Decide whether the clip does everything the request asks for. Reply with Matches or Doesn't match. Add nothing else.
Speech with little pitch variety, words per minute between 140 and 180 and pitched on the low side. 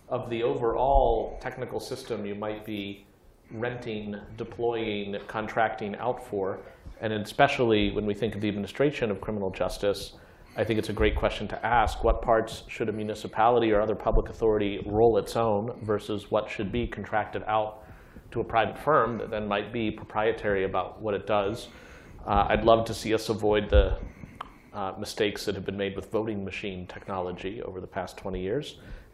Matches